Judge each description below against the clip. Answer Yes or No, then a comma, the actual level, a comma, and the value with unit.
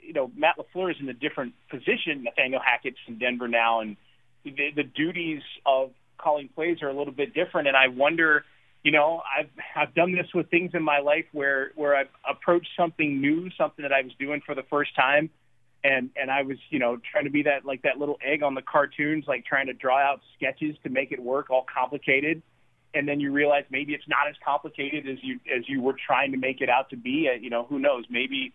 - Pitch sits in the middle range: Yes, medium, 145 Hz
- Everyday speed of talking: No, fast, 230 wpm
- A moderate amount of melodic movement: No, narrow, 2.3 semitones